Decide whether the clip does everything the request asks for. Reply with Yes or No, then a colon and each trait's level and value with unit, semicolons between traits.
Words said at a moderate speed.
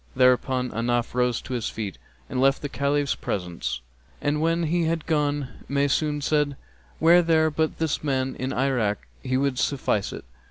Yes: average, 170 wpm